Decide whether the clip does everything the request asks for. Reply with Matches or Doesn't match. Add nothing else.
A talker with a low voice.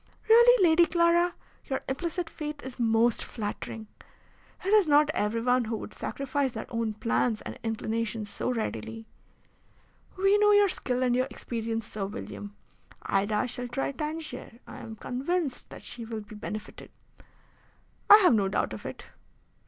Doesn't match